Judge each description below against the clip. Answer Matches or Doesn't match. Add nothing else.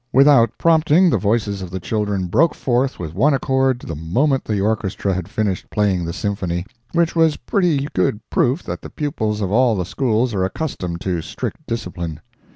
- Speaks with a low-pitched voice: Matches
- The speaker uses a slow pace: Doesn't match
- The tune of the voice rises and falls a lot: Matches